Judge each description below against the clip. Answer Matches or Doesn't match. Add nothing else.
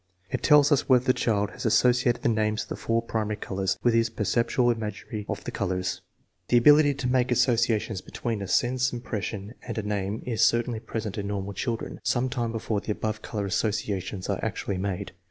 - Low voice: Matches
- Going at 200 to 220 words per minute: Matches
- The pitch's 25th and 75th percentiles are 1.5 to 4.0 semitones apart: Matches